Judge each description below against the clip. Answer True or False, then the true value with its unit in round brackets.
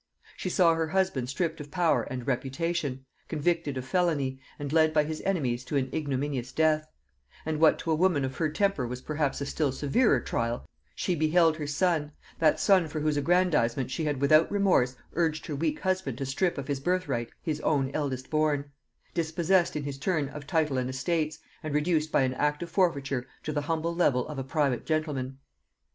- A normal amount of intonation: True (3.4 semitones)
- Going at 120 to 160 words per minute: False (195 wpm)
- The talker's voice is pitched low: False (150 Hz)